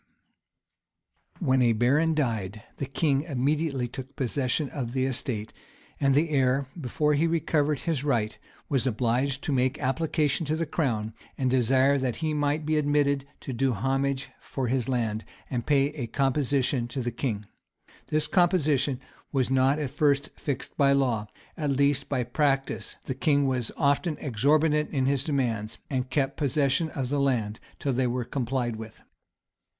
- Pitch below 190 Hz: Yes, low, 135 Hz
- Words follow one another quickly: No, average, 165 wpm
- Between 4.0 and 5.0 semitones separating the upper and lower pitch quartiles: No, average, 2.7 semitones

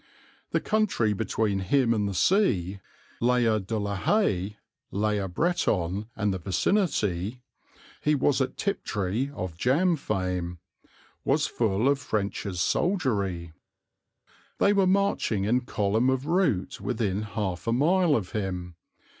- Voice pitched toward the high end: No, low, 110 Hz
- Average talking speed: No, slow, 130 wpm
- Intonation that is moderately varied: No, wide, 6.5 semitones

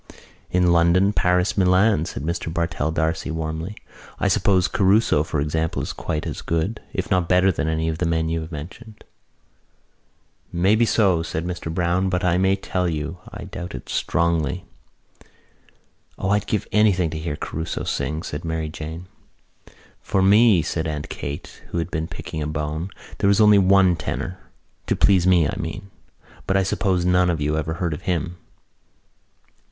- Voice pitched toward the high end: No, very low, 85 Hz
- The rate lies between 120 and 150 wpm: No, average, 170 wpm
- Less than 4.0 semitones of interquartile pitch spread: Yes, average, 2.8 semitones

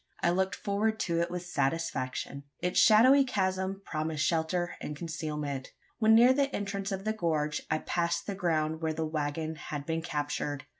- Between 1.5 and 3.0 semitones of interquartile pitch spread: No, average, 4.0 semitones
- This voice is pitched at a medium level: Yes, medium, 170 Hz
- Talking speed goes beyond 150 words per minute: Yes, average, 170 wpm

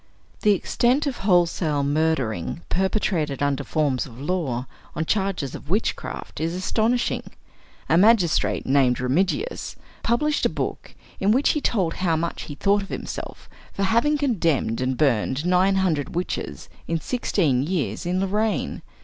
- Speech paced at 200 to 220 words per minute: No, average, 145 wpm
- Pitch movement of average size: No, wide, 6.1 semitones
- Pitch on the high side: No, medium, 175 Hz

